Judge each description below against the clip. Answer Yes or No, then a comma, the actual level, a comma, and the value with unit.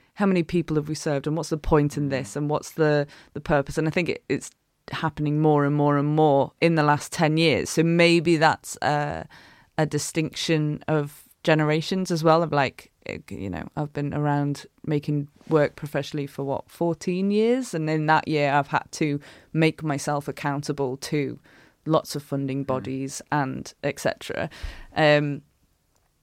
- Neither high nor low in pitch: Yes, medium, 150 Hz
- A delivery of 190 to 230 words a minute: No, average, 170 wpm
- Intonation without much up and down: Yes, narrow, 1.8 semitones